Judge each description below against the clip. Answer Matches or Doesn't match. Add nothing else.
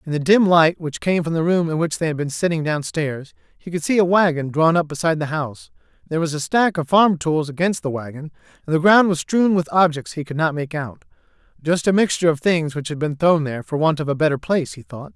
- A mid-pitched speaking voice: Matches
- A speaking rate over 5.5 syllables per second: Matches